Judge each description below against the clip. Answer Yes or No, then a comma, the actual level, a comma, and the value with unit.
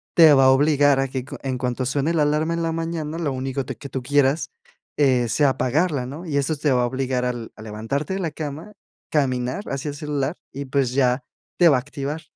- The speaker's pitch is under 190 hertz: Yes, medium, 140 Hz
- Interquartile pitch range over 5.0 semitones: No, average, 2.9 semitones